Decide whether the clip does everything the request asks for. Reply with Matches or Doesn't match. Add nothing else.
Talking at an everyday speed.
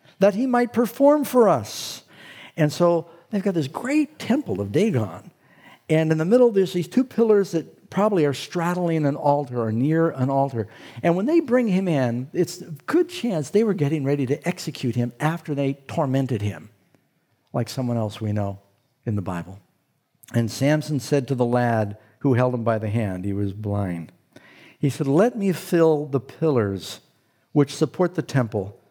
Matches